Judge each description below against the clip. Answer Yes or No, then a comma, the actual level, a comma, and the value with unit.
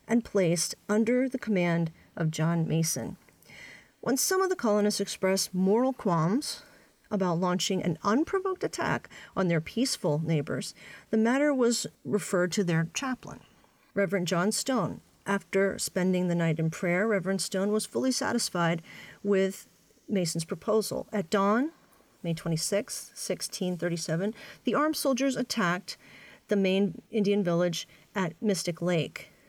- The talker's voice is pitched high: Yes, high, 195 Hz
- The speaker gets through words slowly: Yes, slow, 130 wpm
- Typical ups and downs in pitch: Yes, average, 4.2 semitones